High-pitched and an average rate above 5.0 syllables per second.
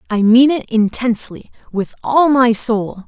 No: high, 235 Hz; 4.4 syllables/s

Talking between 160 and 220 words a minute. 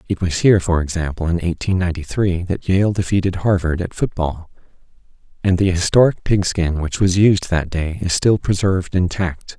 Yes: average, 175 wpm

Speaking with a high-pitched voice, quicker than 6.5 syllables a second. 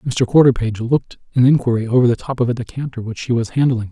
No: low, 125 Hz; 6.7 syllables/s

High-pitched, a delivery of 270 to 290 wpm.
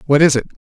No: medium, 140 Hz; fast, 285 wpm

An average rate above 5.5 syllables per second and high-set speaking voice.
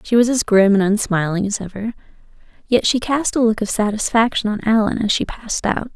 Yes: 5.7 syllables/s; high, 220 Hz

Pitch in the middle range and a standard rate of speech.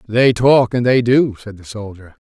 No: low, 115 Hz; average, 185 wpm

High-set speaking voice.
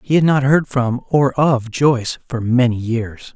No: low, 130 Hz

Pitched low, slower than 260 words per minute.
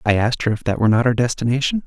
No: low, 120 Hz; fast, 290 wpm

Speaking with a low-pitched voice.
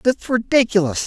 No: high, 215 Hz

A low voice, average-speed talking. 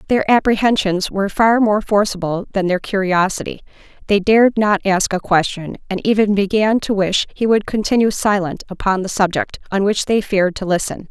No: high, 200 Hz; average, 180 wpm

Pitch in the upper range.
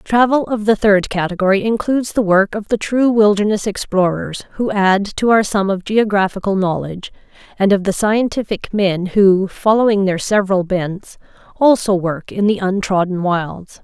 Yes: high, 200 Hz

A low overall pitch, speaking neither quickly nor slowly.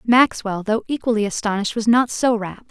No: high, 225 Hz; average, 175 wpm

